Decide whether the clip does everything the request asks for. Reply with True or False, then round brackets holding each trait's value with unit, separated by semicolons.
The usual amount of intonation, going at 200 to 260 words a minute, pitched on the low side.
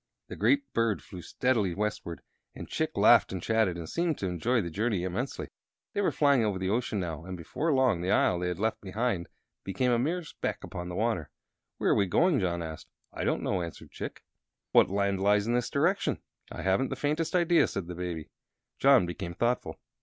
False (5.9 semitones; 205 wpm; 100 Hz)